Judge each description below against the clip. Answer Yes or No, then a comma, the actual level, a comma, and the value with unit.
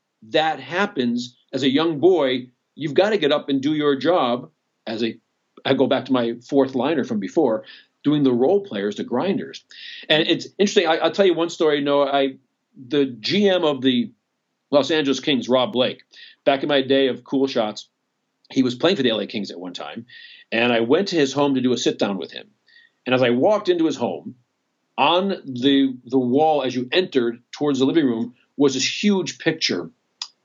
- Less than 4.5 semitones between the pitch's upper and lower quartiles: Yes, average, 4.1 semitones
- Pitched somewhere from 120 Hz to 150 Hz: Yes, medium, 140 Hz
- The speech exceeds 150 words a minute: Yes, fast, 205 wpm